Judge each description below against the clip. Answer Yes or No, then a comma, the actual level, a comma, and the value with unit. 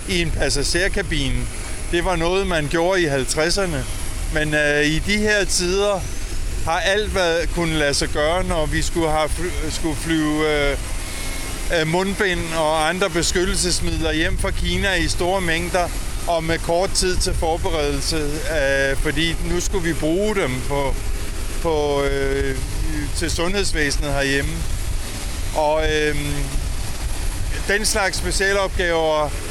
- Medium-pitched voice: Yes, medium, 155 Hz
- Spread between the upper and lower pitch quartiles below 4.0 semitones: No, average, 5.2 semitones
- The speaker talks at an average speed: No, slow, 125 wpm